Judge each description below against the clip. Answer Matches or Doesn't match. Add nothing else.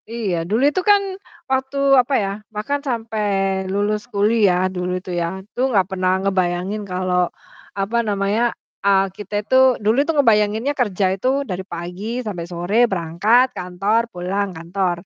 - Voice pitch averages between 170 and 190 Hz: Doesn't match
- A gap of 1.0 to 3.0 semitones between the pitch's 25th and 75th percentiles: Doesn't match